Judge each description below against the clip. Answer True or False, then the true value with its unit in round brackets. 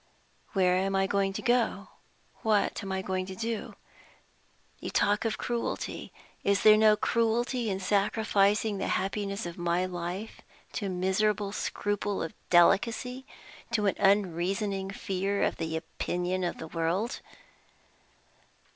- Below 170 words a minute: True (135 wpm)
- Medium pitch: False (195 Hz)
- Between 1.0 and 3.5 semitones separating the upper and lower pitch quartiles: True (2.4 semitones)